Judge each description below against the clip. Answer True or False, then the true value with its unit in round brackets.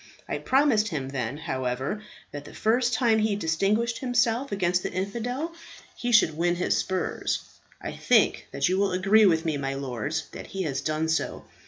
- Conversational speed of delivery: True (180 wpm)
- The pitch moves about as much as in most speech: False (6.3 semitones)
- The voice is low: False (185 Hz)